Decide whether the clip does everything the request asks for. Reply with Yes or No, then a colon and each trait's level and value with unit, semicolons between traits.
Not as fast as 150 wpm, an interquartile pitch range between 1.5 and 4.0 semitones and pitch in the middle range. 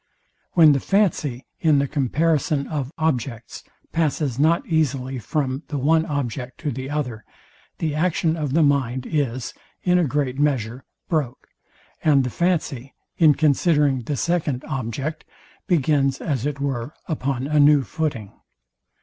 Yes: average, 140 wpm; average, 3.2 semitones; medium, 145 Hz